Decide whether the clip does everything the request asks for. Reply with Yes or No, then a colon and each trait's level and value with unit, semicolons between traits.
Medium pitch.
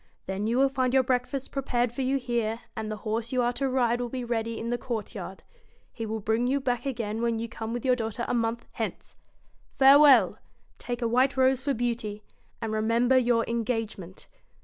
No: high, 240 Hz